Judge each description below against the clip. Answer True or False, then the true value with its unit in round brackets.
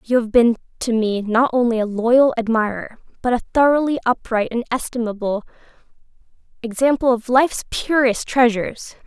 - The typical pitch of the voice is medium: False (235 Hz)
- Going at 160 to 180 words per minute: False (140 wpm)